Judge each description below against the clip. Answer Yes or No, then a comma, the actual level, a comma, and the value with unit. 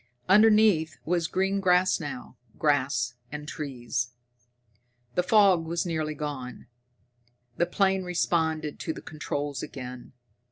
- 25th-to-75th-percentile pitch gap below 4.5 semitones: Yes, average, 4.1 semitones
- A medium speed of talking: No, slow, 115 wpm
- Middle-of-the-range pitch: Yes, medium, 160 Hz